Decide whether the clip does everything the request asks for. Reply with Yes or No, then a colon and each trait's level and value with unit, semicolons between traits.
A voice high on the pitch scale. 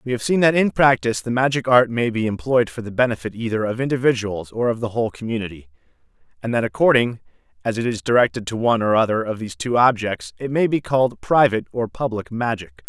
No: low, 115 Hz